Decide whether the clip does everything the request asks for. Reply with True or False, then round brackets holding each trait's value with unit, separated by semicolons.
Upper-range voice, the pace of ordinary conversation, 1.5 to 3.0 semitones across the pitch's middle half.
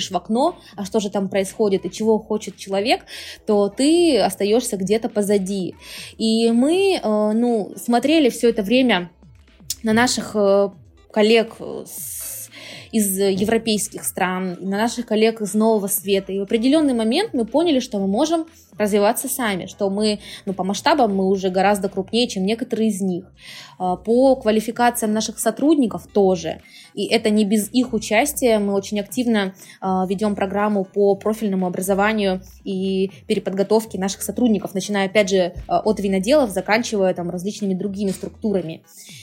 True (210 Hz; 140 wpm; 2.6 semitones)